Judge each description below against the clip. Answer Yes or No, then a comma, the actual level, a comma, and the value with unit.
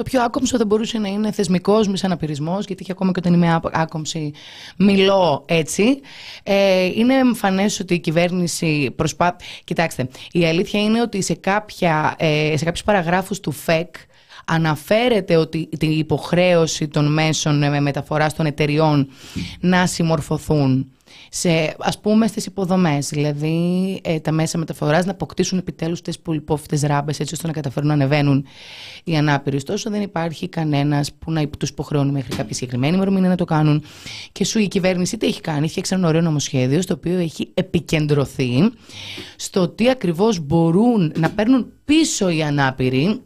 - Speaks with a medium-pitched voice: Yes, medium, 165 Hz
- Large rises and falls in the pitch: No, average, 4.0 semitones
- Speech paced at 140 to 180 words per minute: Yes, average, 160 wpm